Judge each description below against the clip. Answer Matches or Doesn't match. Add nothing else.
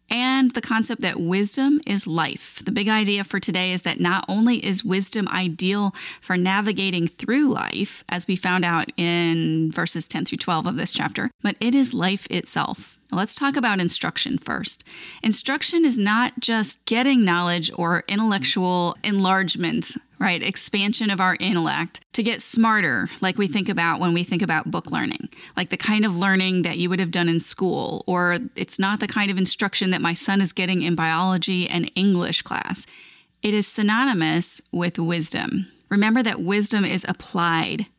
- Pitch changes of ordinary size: Matches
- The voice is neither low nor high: Doesn't match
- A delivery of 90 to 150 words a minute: Doesn't match